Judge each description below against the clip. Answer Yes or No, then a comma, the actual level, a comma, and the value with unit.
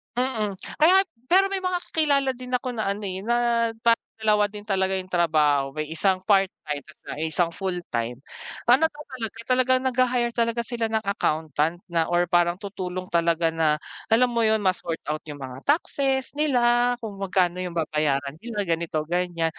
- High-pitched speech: Yes, high, 195 Hz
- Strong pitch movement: Yes, wide, 6.5 semitones